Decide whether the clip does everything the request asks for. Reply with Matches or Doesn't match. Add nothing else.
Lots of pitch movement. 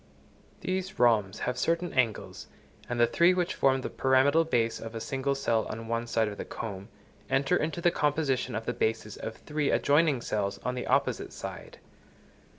Doesn't match